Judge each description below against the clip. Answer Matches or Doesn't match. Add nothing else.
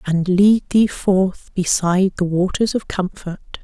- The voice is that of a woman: Matches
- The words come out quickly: Doesn't match